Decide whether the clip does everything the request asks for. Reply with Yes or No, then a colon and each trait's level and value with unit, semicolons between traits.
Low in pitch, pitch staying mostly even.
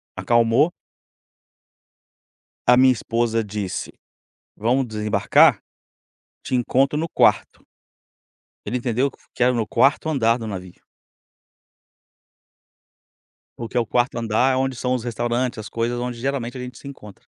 Yes: low, 120 Hz; narrow, 2.1 semitones